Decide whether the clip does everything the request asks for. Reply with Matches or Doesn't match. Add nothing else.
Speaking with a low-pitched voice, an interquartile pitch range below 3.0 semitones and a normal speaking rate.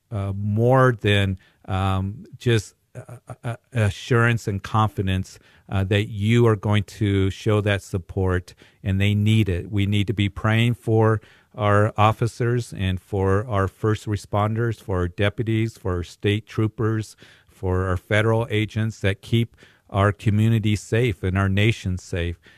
Matches